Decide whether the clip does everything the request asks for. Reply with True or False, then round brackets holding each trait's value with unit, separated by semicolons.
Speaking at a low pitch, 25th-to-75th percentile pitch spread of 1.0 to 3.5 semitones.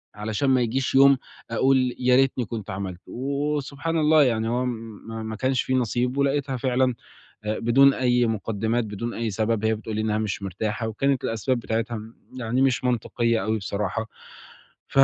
True (120 Hz; 3.0 semitones)